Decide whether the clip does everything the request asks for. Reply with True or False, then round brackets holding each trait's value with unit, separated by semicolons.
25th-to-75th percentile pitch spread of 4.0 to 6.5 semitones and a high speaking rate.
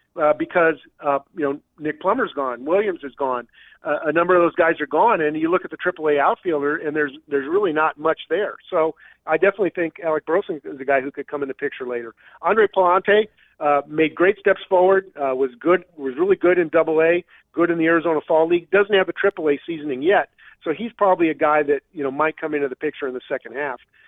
False (3.5 semitones; 235 wpm)